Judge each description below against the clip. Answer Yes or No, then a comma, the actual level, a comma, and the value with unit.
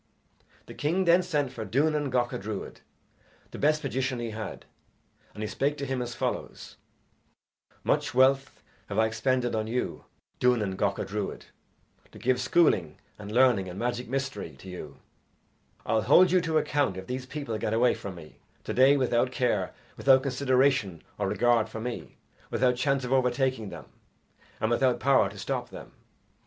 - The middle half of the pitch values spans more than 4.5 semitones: No, average, 3.6 semitones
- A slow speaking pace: No, average, 165 wpm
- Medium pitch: No, low, 125 Hz